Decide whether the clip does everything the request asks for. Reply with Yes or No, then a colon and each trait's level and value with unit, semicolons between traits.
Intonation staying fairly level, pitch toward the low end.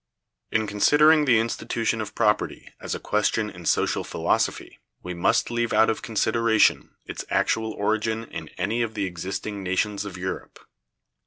Yes: narrow, 2.2 semitones; low, 110 Hz